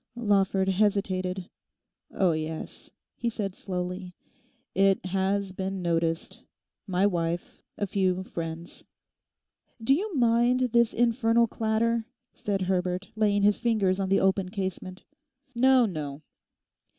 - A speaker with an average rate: No, slow, 115 wpm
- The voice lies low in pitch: No, high, 195 Hz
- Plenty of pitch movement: No, average, 3.4 semitones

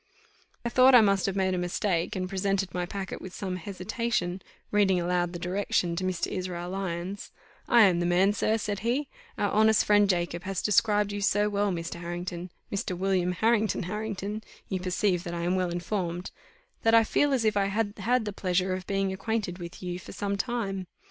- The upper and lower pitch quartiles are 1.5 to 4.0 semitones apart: Yes, narrow, 2.6 semitones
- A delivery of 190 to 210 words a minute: Yes, average, 200 wpm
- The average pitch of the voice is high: Yes, high, 195 Hz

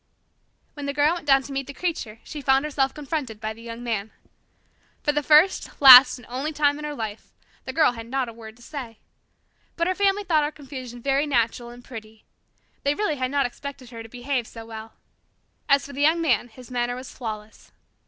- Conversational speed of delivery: No, fast, 210 wpm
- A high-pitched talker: Yes, very high, 265 Hz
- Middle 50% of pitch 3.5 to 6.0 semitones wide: Yes, average, 4.0 semitones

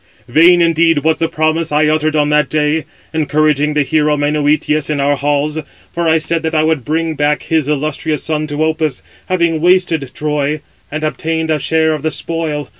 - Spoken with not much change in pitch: Yes, narrow, 1.3 semitones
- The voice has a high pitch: No, medium, 155 Hz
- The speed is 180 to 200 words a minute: Yes, average, 190 wpm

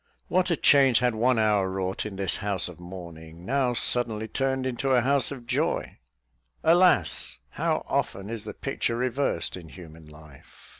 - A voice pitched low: Yes, low, 110 Hz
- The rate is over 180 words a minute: No, average, 165 wpm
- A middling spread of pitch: No, wide, 5.8 semitones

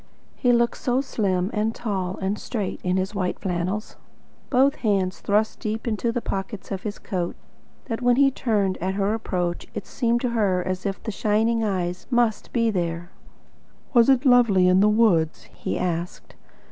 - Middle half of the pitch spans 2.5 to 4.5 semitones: Yes, average, 3.9 semitones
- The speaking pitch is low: No, high, 210 Hz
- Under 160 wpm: No, average, 175 wpm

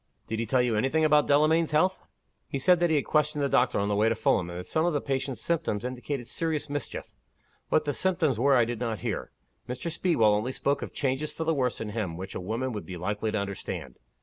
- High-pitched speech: No, low, 130 Hz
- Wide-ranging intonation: Yes, wide, 5.7 semitones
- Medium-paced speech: No, fast, 255 wpm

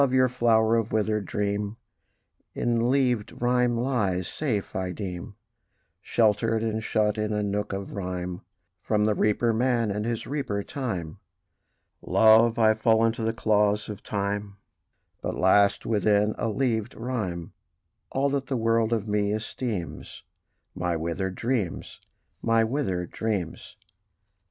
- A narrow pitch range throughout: Yes, narrow, 2.3 semitones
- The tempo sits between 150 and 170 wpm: No, slow, 135 wpm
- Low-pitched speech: Yes, low, 110 Hz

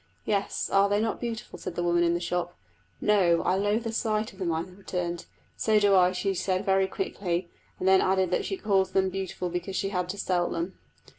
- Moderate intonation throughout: No, narrow, 2.3 semitones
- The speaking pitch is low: No, high, 190 Hz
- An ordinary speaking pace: No, fast, 220 wpm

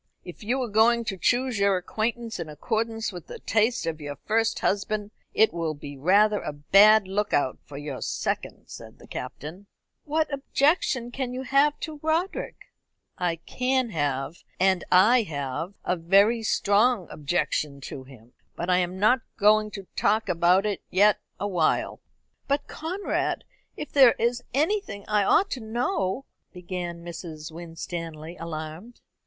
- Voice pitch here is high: Yes, high, 200 Hz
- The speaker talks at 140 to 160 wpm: Yes, average, 155 wpm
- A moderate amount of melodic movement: No, wide, 6.0 semitones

